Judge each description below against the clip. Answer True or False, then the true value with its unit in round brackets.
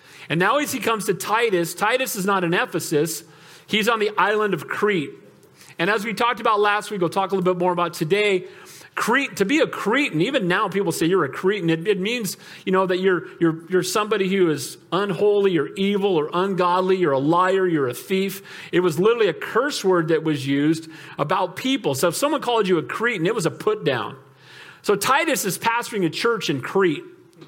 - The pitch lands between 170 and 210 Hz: True (190 Hz)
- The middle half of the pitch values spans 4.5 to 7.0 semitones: False (3.7 semitones)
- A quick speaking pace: True (215 wpm)